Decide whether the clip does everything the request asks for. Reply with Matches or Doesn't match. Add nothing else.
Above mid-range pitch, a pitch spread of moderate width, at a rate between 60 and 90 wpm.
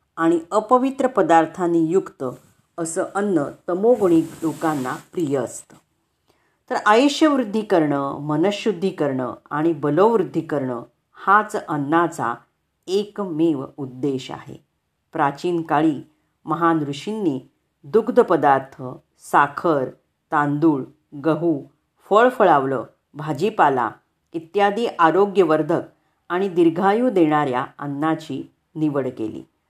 Doesn't match